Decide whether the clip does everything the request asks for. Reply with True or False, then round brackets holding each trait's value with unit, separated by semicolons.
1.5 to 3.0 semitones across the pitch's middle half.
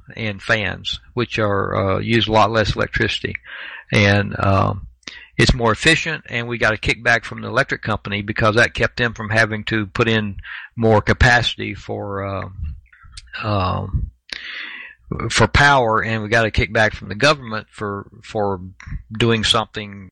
True (2.5 semitones)